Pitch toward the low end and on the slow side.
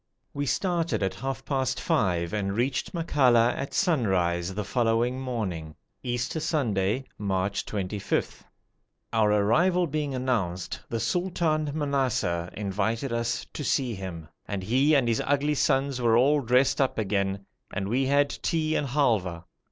No: low, 120 Hz; average, 145 wpm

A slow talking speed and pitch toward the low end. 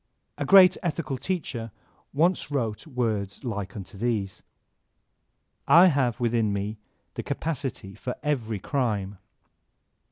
Yes: slow, 115 wpm; low, 120 Hz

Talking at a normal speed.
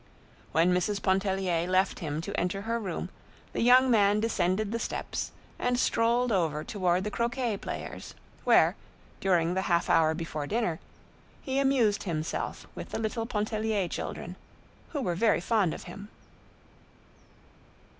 Yes: average, 145 wpm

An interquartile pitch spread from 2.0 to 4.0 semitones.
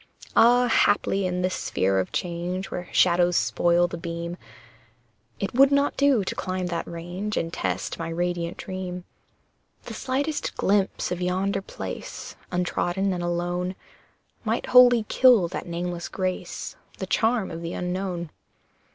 Yes: narrow, 2.5 semitones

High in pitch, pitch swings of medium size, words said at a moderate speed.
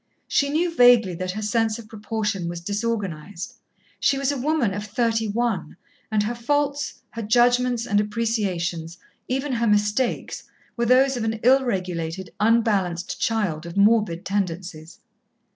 Yes: high, 220 Hz; average, 4.3 semitones; average, 145 wpm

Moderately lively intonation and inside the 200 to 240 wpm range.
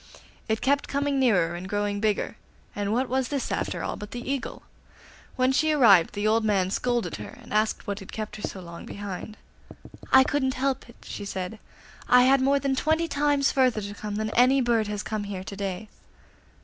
Yes: average, 4.5 semitones; fast, 205 wpm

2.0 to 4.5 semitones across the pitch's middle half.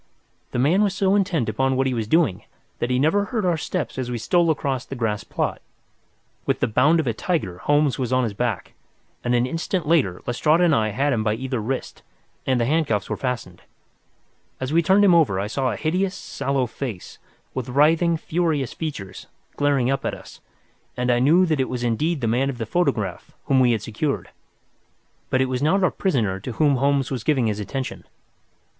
No: average, 5.1 semitones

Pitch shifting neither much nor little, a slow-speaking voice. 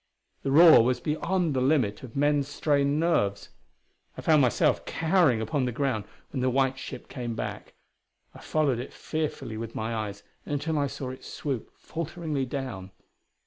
No: average, 3.9 semitones; average, 165 wpm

